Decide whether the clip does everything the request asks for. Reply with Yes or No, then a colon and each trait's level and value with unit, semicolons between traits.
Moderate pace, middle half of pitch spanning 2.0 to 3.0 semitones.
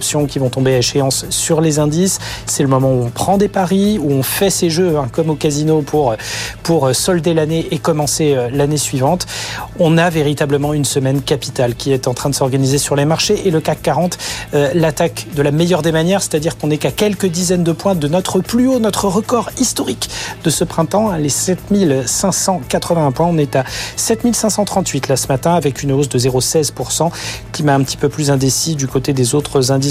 No: average, 210 wpm; average, 4.5 semitones